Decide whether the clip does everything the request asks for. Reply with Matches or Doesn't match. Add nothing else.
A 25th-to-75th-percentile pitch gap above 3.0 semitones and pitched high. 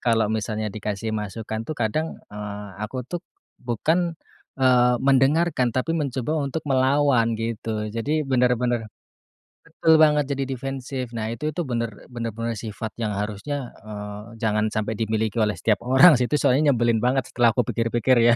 Doesn't match